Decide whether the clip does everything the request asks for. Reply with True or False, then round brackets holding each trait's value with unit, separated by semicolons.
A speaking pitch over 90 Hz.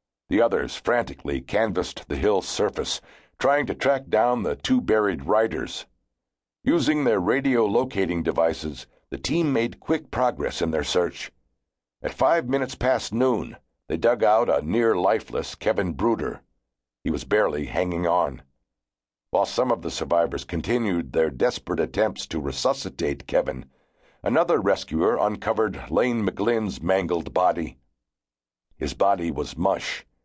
False (70 Hz)